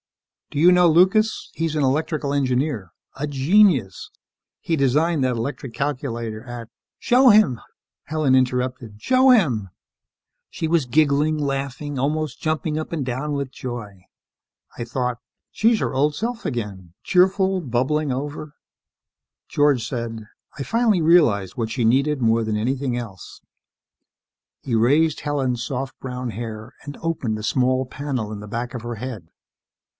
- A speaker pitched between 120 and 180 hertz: Yes, low, 135 Hz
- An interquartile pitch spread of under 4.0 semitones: No, average, 4.5 semitones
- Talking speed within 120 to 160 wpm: Yes, average, 150 wpm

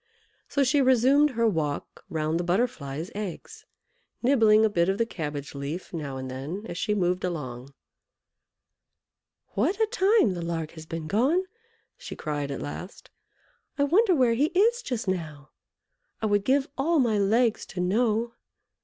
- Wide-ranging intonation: Yes, wide, 8.4 semitones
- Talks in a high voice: Yes, high, 205 Hz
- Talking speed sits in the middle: Yes, average, 160 wpm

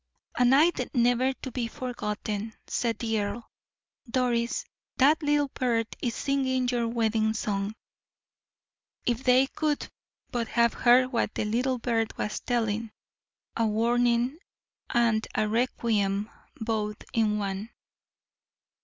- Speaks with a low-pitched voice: No, high, 235 Hz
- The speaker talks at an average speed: No, slow, 120 wpm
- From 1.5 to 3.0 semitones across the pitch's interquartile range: Yes, narrow, 2.6 semitones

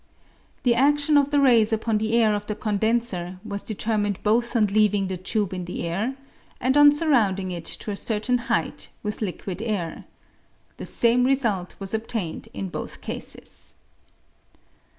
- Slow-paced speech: No, average, 165 wpm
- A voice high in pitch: Yes, high, 215 Hz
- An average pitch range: Yes, average, 3.5 semitones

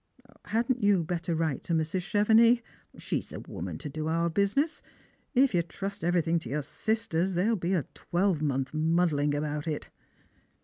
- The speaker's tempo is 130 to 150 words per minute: No, average, 160 wpm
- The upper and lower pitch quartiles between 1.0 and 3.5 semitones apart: No, average, 4.6 semitones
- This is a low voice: No, medium, 170 Hz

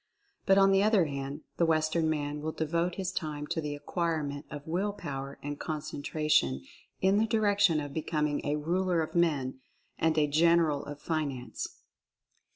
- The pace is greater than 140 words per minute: Yes, average, 165 wpm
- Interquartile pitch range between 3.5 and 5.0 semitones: No, average, 2.9 semitones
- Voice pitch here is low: No, medium, 155 Hz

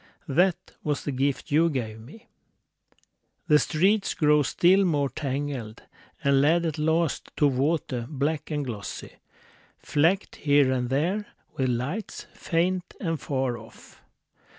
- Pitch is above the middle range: No, medium, 145 Hz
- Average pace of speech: No, slow, 130 wpm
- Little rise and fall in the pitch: No, average, 4.1 semitones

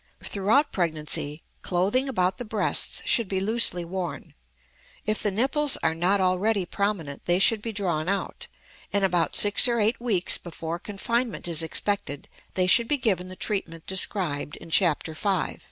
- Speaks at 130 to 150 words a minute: No, average, 160 wpm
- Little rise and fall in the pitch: No, average, 3.7 semitones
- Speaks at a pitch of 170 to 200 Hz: Yes, high, 190 Hz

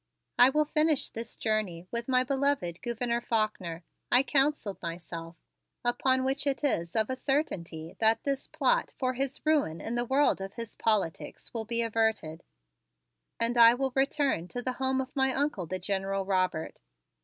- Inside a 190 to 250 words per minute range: No, average, 165 wpm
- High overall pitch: Yes, high, 235 Hz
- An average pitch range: No, wide, 5.7 semitones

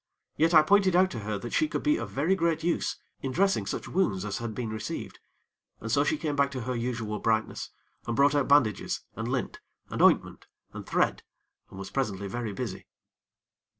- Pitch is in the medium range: No, low, 130 Hz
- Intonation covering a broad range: Yes, wide, 6.6 semitones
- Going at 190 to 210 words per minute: Yes, average, 200 wpm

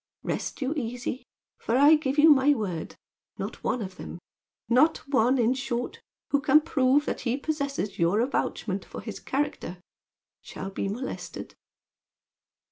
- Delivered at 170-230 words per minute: No, average, 145 wpm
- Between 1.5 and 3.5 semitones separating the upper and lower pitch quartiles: No, average, 4.0 semitones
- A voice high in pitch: Yes, very high, 260 Hz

